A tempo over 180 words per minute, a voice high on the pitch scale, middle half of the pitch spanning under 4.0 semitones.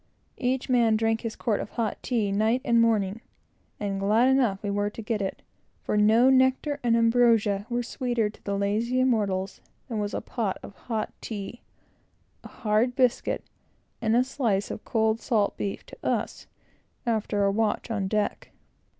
No: average, 170 wpm; high, 225 Hz; average, 2.8 semitones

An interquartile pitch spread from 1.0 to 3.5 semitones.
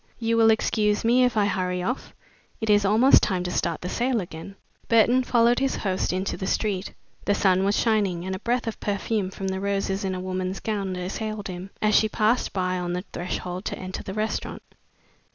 Yes: average, 3.1 semitones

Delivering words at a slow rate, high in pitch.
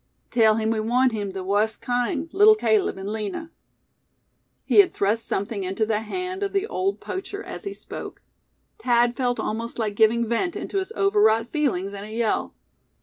No: average, 180 wpm; high, 235 Hz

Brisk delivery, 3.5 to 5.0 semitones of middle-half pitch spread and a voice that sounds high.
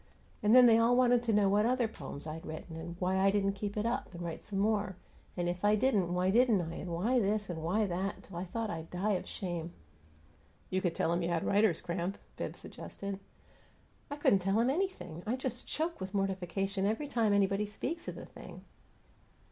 Yes: fast, 215 wpm; average, 4.0 semitones; high, 195 Hz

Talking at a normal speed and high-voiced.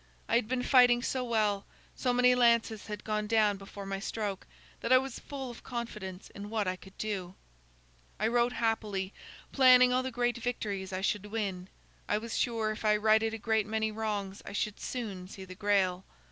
Yes: average, 195 wpm; high, 215 Hz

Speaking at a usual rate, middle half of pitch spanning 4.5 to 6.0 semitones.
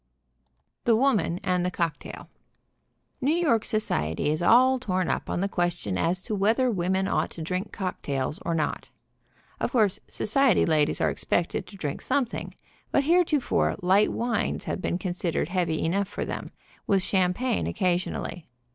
Yes: average, 155 wpm; average, 4.8 semitones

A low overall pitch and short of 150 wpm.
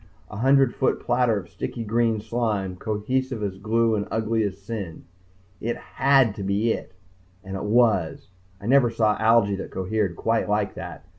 No: low, 110 Hz; average, 170 wpm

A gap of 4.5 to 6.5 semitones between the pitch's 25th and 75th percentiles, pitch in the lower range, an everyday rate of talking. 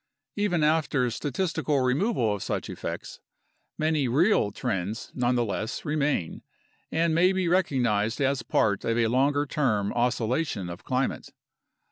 No: wide, 5.5 semitones; low, 130 Hz; slow, 125 wpm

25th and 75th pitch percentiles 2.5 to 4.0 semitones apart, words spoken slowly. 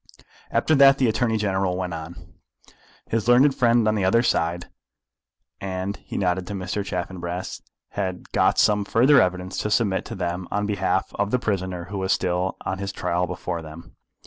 No: average, 2.9 semitones; average, 175 wpm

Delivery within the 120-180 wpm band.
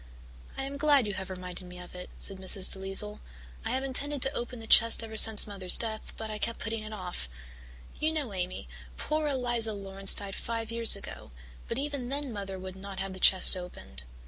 No: fast, 205 wpm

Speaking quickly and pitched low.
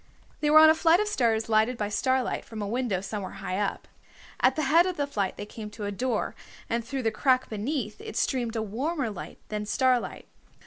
No: fast, 220 wpm; high, 235 Hz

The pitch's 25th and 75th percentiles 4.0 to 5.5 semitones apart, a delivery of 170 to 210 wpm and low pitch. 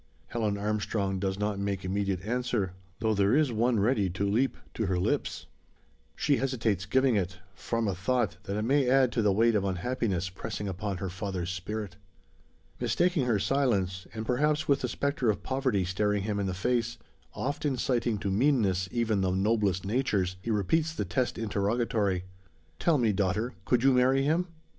Yes: average, 4.5 semitones; average, 175 wpm; low, 105 Hz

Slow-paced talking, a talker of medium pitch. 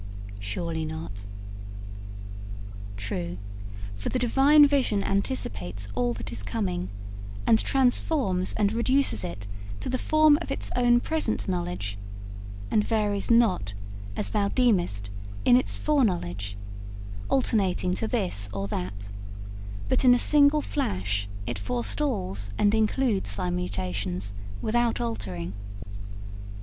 Yes: slow, 115 wpm; medium, 180 Hz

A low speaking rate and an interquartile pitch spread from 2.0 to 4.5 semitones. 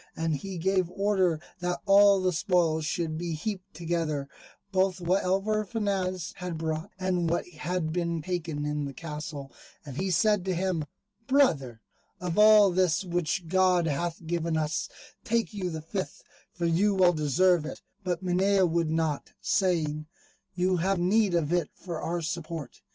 No: average, 160 wpm; average, 2.9 semitones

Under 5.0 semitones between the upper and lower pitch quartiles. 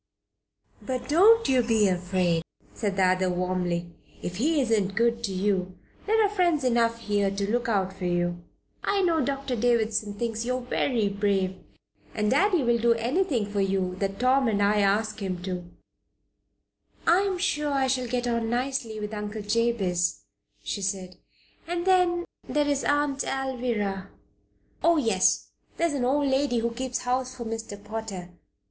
No: average, 5.3 semitones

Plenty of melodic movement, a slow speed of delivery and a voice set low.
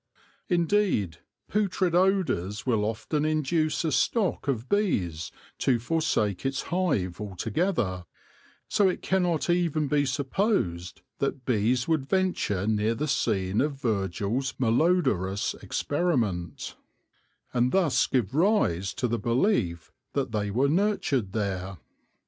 Yes: wide, 8.6 semitones; slow, 120 wpm; low, 130 Hz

